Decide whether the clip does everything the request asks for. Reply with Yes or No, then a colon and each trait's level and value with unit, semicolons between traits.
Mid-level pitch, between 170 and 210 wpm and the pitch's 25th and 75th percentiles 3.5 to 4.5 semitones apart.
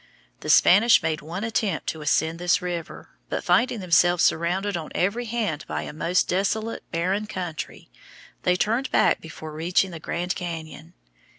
No: medium, 180 Hz; average, 160 wpm; average, 3.8 semitones